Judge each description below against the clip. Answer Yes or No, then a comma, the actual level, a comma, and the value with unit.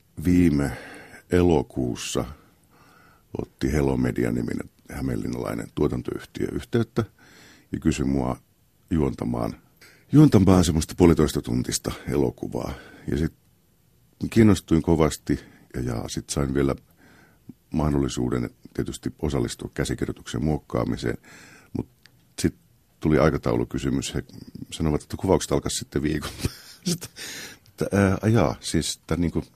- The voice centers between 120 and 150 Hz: No, very low, 80 Hz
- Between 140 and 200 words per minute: No, slow, 95 wpm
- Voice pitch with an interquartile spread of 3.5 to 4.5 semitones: No, average, 5.1 semitones